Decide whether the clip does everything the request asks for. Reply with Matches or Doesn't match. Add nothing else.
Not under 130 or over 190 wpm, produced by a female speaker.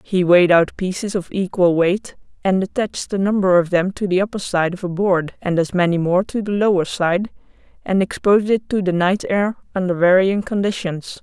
Doesn't match